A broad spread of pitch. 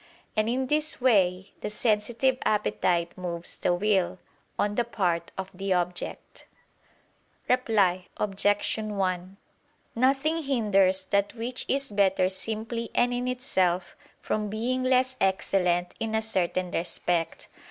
No: average, 4.7 semitones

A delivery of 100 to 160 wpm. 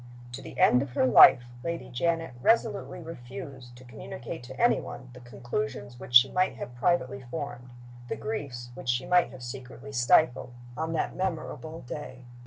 No: average, 170 wpm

